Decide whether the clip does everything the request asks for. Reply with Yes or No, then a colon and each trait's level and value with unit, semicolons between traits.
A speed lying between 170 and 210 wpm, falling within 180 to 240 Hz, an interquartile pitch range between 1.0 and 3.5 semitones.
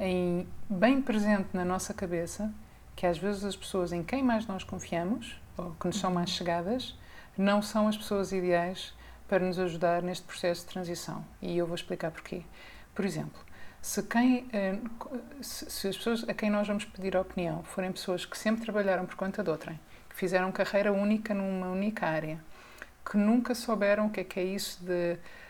Yes: fast, 185 wpm; high, 190 Hz; average, 2.8 semitones